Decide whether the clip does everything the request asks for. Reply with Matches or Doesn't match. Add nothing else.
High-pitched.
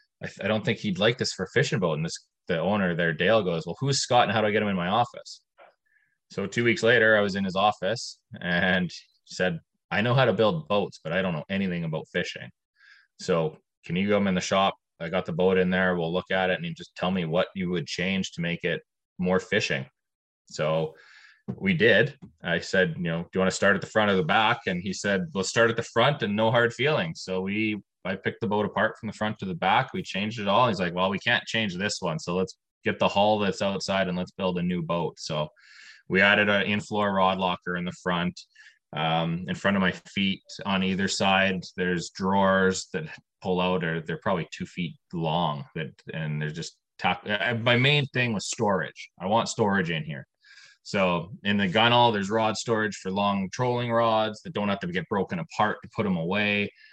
Doesn't match